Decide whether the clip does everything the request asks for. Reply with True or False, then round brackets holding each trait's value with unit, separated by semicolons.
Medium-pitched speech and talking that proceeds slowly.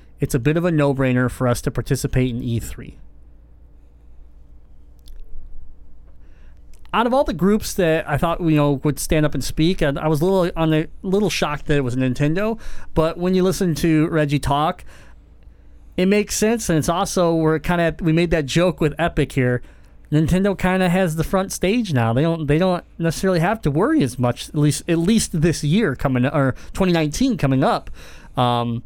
False (150 Hz; 200 wpm)